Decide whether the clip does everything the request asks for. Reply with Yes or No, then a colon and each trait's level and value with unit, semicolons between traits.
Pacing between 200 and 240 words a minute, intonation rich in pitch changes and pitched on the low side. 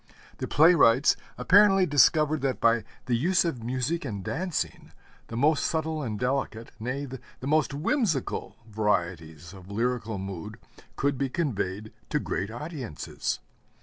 No: slow, 135 wpm; wide, 6.2 semitones; low, 130 Hz